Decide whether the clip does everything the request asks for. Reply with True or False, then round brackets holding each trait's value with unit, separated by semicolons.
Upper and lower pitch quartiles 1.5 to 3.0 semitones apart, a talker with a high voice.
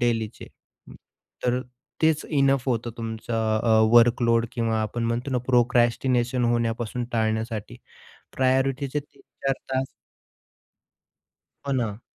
False (2.4 semitones; 120 Hz)